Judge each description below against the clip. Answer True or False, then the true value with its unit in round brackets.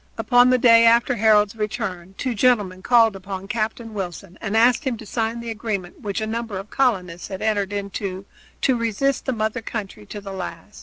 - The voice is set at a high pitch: True (215 Hz)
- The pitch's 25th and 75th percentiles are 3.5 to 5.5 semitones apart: False (3.1 semitones)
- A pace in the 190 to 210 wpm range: True (195 wpm)